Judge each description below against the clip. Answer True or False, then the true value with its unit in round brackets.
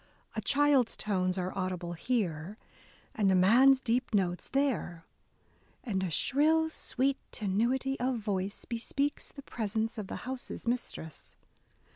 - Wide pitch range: True (5.9 semitones)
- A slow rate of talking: True (130 wpm)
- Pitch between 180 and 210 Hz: False (225 Hz)